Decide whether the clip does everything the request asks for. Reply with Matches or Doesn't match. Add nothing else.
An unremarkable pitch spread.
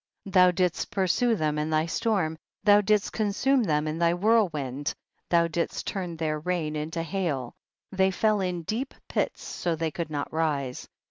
Matches